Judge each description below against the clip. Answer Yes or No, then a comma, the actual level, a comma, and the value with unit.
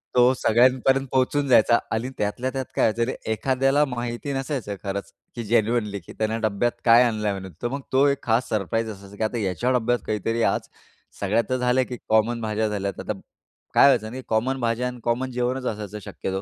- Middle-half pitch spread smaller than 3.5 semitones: Yes, average, 2.9 semitones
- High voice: No, low, 120 Hz